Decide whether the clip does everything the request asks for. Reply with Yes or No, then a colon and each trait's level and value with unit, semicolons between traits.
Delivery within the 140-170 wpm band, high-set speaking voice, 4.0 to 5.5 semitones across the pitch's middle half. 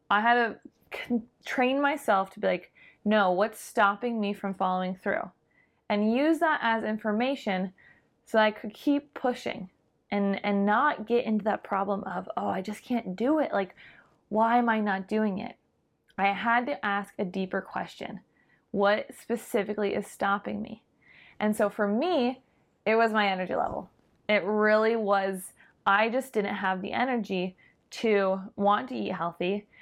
No: average, 165 wpm; high, 210 Hz; average, 3.0 semitones